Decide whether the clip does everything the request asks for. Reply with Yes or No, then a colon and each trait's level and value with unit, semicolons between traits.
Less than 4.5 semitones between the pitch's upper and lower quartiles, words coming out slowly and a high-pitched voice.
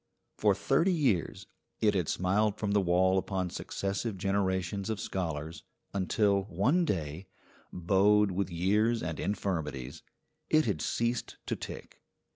No: average, 2.9 semitones; slow, 130 wpm; very low, 95 Hz